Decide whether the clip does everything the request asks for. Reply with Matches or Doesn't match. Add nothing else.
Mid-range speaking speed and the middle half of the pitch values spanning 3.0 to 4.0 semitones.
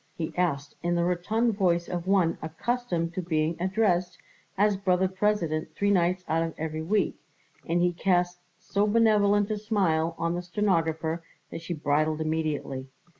Matches